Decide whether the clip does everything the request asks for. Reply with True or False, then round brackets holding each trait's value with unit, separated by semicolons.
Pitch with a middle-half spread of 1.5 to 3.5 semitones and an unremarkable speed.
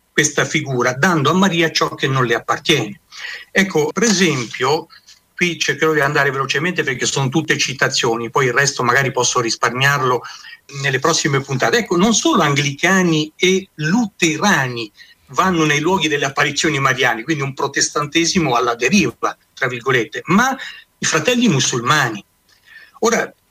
False (4.2 semitones; 140 wpm)